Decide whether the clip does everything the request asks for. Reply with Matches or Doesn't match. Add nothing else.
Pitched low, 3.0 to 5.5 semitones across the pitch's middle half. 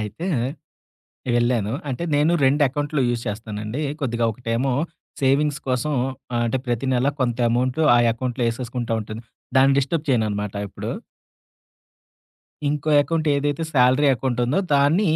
Matches